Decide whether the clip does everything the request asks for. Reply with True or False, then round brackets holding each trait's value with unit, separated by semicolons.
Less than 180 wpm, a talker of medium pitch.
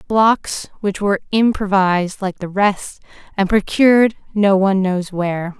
False (140 wpm; 195 Hz)